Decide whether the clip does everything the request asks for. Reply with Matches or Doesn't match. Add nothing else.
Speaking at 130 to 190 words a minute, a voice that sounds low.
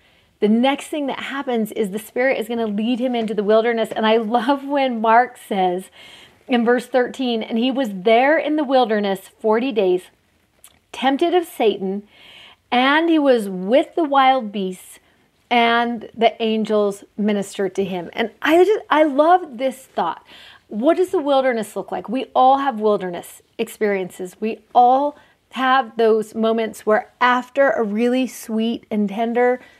Doesn't match